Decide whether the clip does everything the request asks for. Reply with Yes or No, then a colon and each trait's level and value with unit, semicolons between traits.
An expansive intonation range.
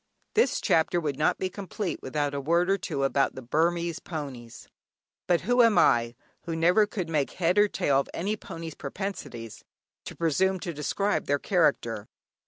No: average, 5.0 semitones